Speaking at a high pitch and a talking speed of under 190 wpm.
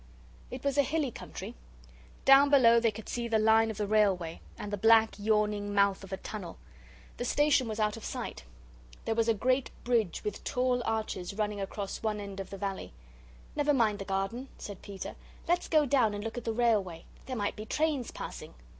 No: high, 220 Hz; average, 200 wpm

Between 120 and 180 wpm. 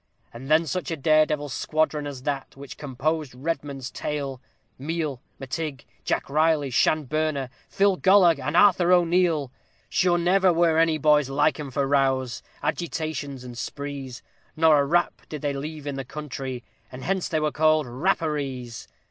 Yes: average, 160 wpm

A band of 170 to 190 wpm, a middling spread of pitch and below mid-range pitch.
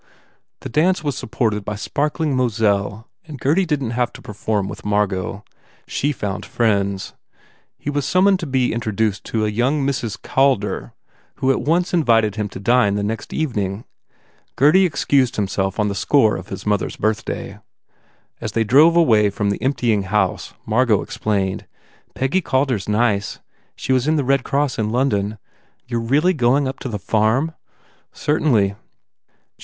Yes: average, 175 wpm; average, 5.0 semitones; low, 115 Hz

